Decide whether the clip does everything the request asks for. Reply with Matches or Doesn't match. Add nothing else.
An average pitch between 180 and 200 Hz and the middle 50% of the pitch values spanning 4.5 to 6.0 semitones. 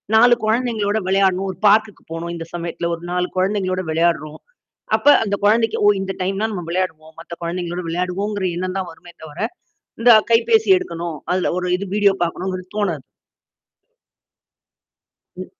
Doesn't match